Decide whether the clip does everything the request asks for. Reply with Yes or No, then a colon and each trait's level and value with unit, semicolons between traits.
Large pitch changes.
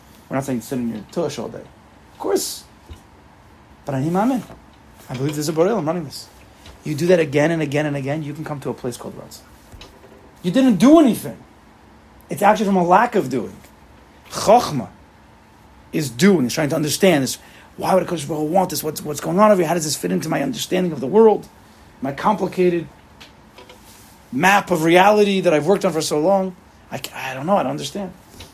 Yes: wide, 5.8 semitones